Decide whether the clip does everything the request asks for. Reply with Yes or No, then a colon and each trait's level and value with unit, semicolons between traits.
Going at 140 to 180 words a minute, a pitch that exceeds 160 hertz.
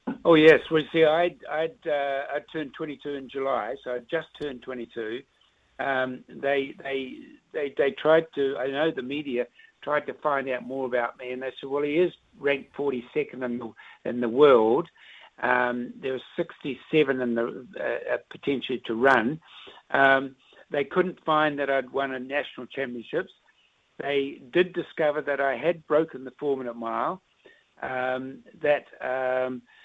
No: average, 170 wpm; medium, 140 Hz